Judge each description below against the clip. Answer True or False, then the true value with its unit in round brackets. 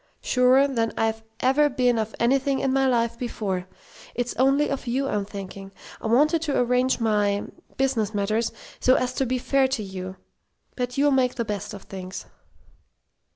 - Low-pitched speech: False (245 Hz)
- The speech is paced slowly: False (170 wpm)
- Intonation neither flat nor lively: True (4.0 semitones)